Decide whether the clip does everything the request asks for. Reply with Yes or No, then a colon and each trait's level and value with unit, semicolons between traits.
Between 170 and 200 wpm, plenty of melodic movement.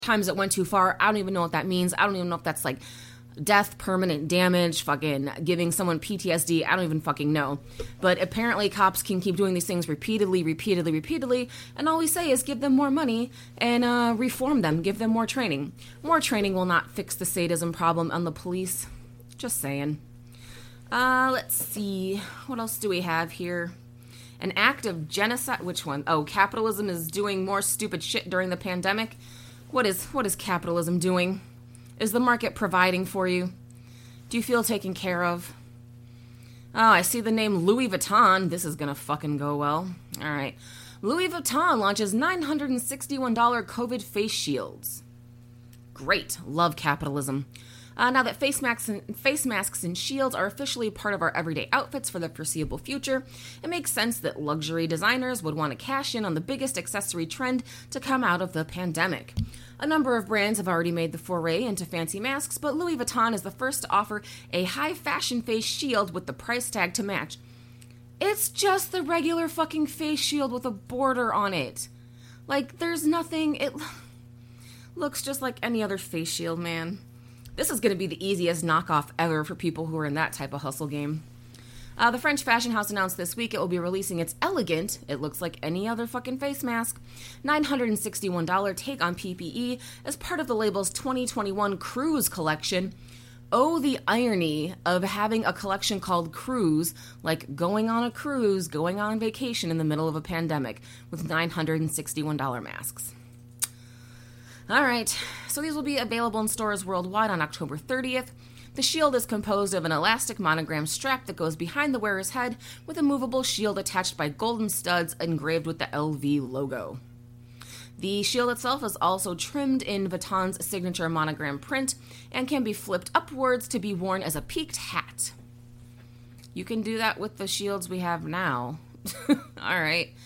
Yes: average, 180 wpm; wide, 7.6 semitones